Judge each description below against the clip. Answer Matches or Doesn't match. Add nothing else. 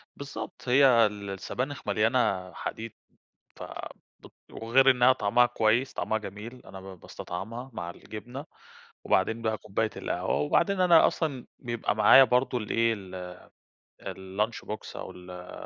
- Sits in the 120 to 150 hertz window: Doesn't match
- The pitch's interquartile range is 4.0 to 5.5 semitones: Matches